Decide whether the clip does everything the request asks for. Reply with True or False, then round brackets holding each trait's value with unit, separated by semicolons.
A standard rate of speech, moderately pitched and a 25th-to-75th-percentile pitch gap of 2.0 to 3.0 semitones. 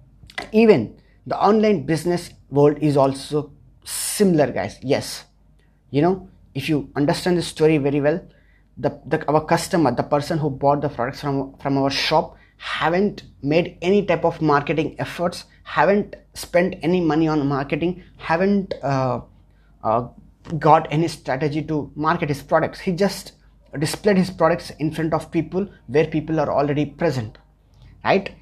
False (150 wpm; 155 Hz; 3.4 semitones)